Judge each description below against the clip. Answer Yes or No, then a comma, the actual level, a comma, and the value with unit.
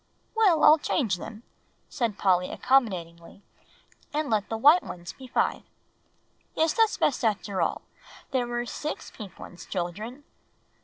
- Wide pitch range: Yes, wide, 7.4 semitones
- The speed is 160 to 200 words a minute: No, average, 140 wpm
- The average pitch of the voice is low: No, high, 225 Hz